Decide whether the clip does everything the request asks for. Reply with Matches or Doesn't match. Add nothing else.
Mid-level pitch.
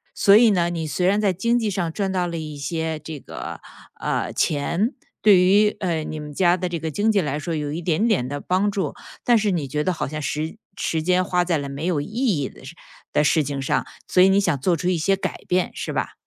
Matches